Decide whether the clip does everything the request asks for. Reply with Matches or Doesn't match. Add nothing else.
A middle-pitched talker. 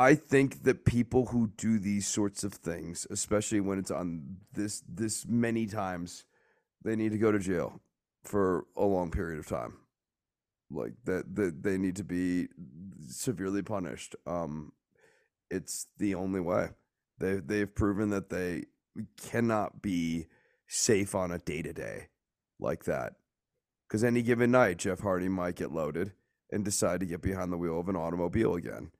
Doesn't match